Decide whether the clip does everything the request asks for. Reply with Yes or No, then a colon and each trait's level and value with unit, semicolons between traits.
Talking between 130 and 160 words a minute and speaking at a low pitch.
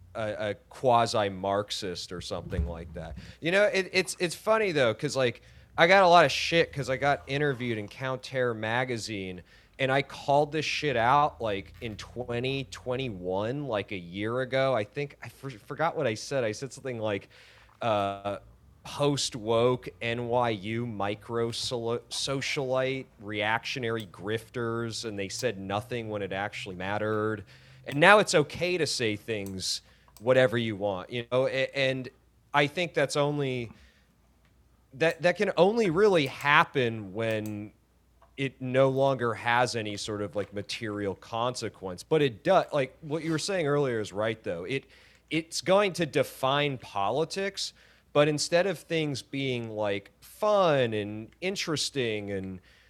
Yes: average, 150 wpm; low, 120 Hz